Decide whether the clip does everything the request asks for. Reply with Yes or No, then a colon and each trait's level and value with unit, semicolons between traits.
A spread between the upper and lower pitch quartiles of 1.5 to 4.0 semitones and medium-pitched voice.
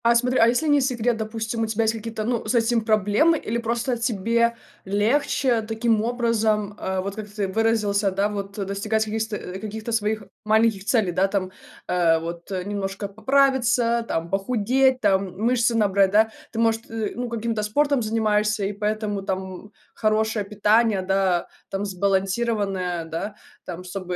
No: average, 2.7 semitones; high, 215 Hz